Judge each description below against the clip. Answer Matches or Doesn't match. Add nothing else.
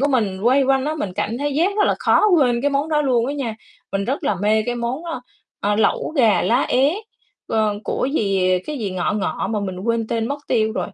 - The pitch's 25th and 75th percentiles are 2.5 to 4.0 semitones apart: Doesn't match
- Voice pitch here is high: Matches